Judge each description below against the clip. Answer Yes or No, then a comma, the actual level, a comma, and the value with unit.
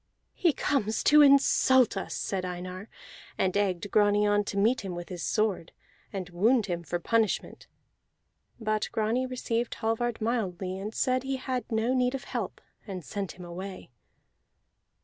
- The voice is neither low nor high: No, high, 215 Hz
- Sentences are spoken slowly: No, average, 155 wpm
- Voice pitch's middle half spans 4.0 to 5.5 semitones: Yes, average, 4.5 semitones